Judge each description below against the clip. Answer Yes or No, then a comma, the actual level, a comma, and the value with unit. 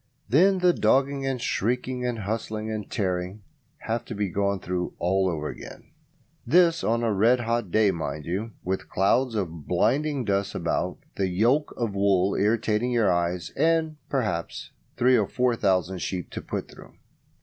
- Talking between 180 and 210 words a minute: No, average, 165 wpm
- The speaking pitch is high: No, low, 110 Hz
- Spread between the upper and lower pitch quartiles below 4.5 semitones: No, average, 4.8 semitones